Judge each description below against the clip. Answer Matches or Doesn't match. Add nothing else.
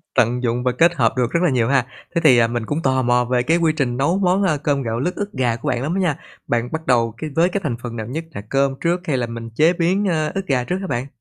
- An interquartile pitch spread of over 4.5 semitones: Matches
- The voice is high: Doesn't match